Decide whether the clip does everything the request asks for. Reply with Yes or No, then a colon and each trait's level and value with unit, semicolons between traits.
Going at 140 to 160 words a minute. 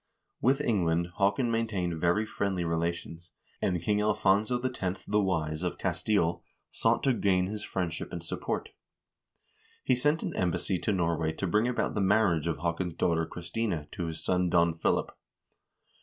Yes: average, 155 wpm